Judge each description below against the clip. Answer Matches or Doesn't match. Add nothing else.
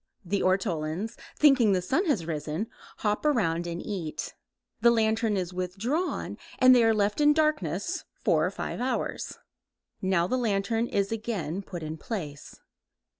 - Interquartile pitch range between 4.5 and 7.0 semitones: Matches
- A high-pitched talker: Matches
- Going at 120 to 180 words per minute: Matches